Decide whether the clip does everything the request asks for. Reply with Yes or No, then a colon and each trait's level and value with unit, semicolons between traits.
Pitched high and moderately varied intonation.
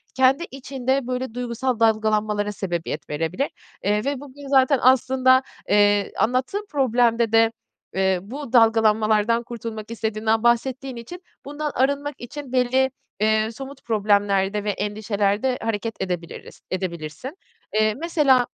Yes: high, 230 Hz; average, 3.9 semitones